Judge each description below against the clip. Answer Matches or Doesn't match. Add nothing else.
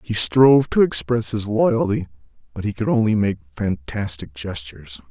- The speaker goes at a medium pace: Matches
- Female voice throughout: Doesn't match